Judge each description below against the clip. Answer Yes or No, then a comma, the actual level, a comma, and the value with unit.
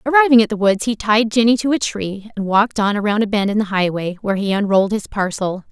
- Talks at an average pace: No, fast, 250 wpm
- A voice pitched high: Yes, high, 210 Hz